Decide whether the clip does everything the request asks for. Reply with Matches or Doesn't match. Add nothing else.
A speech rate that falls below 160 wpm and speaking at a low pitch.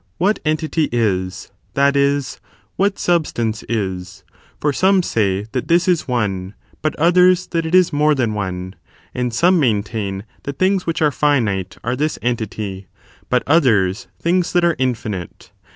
Matches